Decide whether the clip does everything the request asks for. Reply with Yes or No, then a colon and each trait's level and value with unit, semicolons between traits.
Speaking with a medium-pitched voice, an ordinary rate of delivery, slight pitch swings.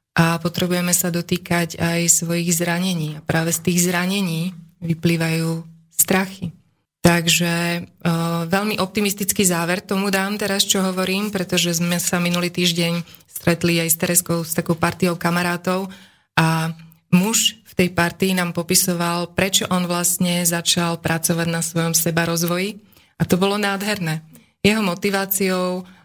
Yes: medium, 175 Hz; average, 135 wpm; narrow, 1.7 semitones